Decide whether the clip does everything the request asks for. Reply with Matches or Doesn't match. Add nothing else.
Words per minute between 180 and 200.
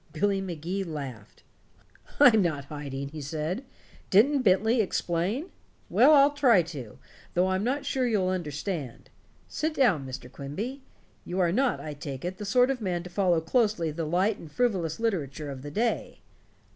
Doesn't match